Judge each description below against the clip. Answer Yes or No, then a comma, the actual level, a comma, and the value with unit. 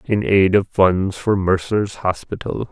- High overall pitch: No, very low, 95 Hz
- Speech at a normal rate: Yes, average, 155 wpm